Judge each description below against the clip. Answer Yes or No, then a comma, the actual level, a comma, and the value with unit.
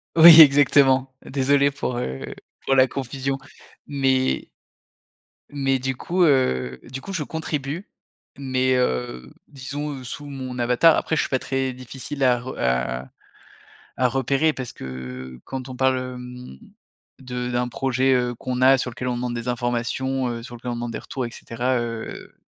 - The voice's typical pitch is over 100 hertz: Yes, low, 130 Hz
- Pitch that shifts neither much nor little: No, narrow, 2.0 semitones